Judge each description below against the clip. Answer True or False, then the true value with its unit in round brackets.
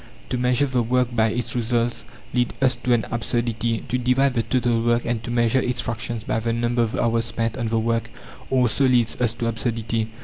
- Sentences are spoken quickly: True (210 wpm)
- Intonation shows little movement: True (1.3 semitones)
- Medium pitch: False (120 Hz)